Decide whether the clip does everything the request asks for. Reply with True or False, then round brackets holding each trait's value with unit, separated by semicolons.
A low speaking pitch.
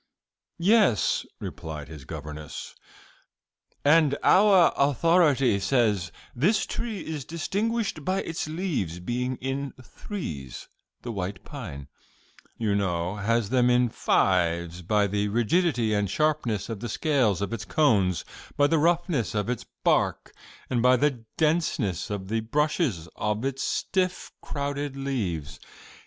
True (120 Hz)